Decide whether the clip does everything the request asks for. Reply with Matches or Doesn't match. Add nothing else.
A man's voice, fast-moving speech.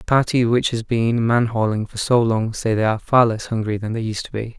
Matches